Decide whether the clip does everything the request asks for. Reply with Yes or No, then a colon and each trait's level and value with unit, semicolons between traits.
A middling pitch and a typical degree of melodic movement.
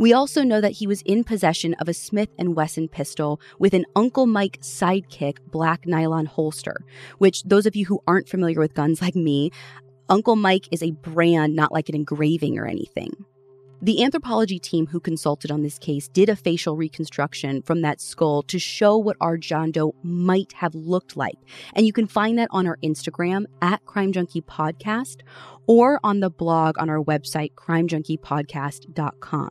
Yes: medium, 165 Hz; average, 4.2 semitones